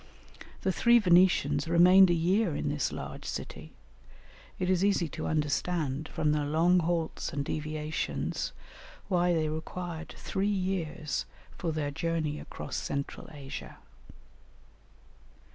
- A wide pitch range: No, average, 3.0 semitones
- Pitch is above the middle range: No, medium, 165 Hz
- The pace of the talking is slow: Yes, slow, 125 wpm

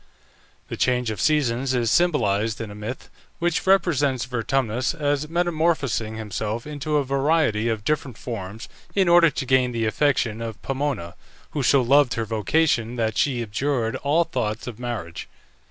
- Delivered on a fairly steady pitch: No, average, 4.7 semitones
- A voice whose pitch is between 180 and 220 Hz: No, low, 125 Hz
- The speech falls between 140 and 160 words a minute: Yes, average, 155 wpm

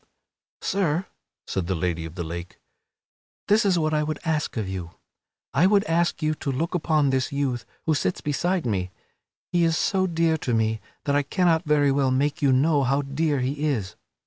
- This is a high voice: No, medium, 145 Hz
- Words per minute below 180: No, average, 195 wpm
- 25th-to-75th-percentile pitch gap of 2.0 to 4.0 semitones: No, average, 4.8 semitones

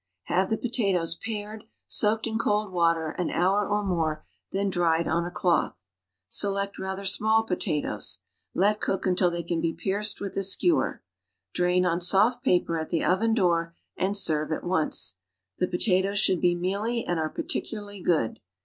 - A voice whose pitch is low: No, high, 190 Hz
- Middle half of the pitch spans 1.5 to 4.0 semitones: Yes, average, 3.3 semitones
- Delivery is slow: No, average, 170 wpm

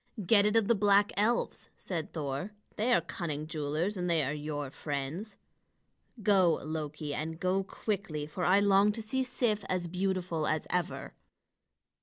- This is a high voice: No, medium, 180 Hz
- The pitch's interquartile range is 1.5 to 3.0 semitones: No, average, 4.8 semitones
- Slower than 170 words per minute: Yes, average, 160 wpm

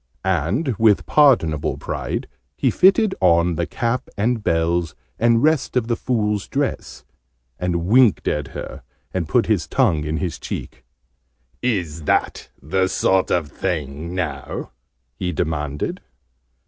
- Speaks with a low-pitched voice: Yes, very low, 95 Hz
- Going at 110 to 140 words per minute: Yes, slow, 135 wpm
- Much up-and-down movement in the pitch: Yes, wide, 6.3 semitones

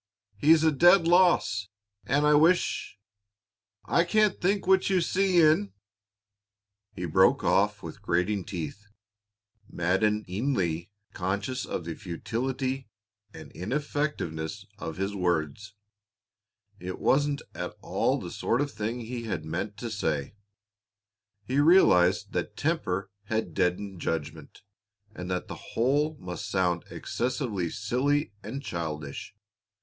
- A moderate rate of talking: No, slow, 125 wpm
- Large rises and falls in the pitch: Yes, wide, 8.0 semitones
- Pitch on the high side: No, low, 105 Hz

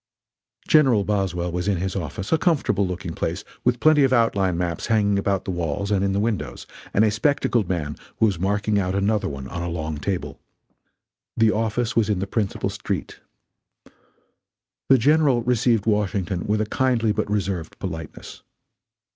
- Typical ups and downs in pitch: Yes, average, 3.9 semitones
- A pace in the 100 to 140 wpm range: No, average, 165 wpm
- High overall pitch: No, low, 100 Hz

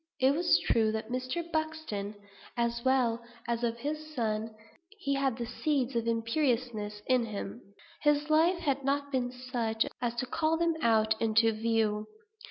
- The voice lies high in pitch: Yes, high, 245 Hz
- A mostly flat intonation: No, average, 4.2 semitones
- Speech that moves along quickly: No, average, 165 wpm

